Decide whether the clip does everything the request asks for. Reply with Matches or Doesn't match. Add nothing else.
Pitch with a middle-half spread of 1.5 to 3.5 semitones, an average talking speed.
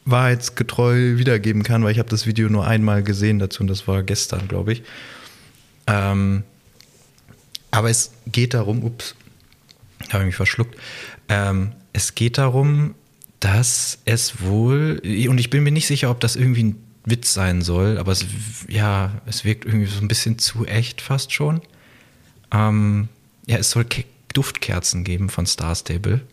Matches